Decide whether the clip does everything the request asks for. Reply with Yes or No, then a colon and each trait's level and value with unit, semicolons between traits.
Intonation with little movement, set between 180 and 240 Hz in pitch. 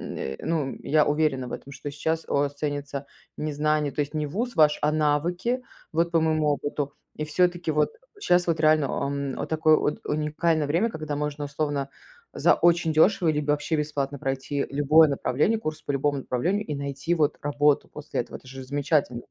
No: narrow, 2.0 semitones; medium, 150 Hz